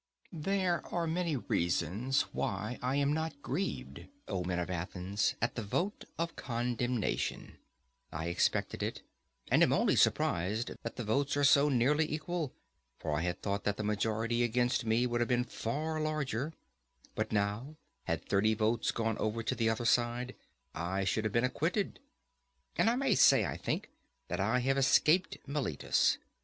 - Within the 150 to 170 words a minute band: Yes, average, 165 wpm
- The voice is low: Yes, low, 120 Hz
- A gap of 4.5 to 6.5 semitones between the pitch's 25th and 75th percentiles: Yes, wide, 5.5 semitones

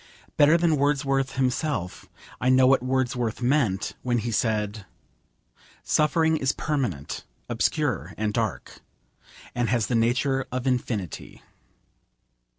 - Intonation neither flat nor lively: Yes, average, 3.3 semitones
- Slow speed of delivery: Yes, slow, 115 wpm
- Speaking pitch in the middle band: No, low, 125 Hz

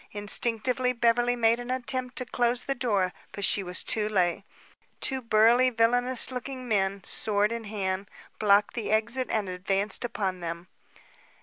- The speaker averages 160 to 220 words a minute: No, average, 150 wpm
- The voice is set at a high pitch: Yes, high, 225 Hz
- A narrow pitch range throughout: No, average, 3.6 semitones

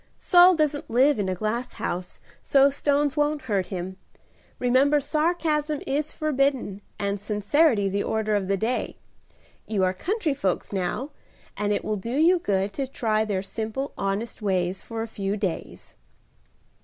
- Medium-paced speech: Yes, average, 155 wpm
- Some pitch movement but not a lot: No, wide, 6.5 semitones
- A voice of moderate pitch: No, high, 225 Hz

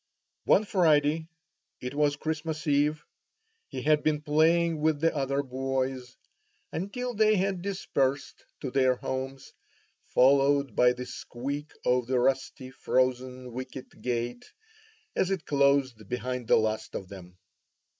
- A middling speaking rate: No, slow, 130 wpm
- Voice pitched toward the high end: No, medium, 140 Hz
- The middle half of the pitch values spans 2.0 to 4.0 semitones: Yes, average, 3.5 semitones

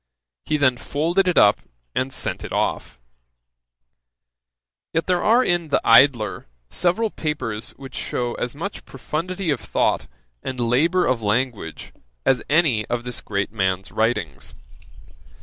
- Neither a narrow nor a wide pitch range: No, wide, 6.4 semitones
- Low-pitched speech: Yes, low, 130 Hz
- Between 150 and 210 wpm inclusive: No, slow, 135 wpm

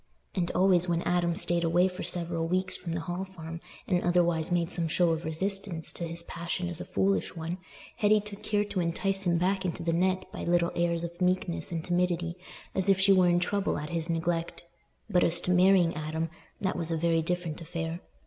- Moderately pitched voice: Yes, medium, 175 Hz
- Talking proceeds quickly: Yes, fast, 210 wpm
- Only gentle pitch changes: Yes, narrow, 1.8 semitones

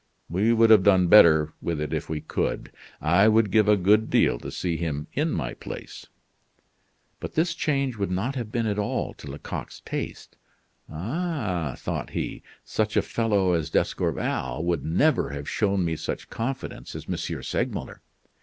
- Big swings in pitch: Yes, wide, 5.8 semitones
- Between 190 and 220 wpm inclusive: No, average, 170 wpm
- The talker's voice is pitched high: No, low, 100 Hz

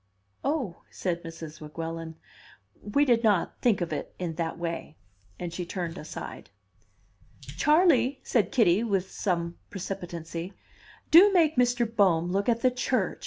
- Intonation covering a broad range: Yes, wide, 6.4 semitones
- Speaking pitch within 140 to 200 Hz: Yes, high, 190 Hz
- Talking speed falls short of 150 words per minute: Yes, average, 140 wpm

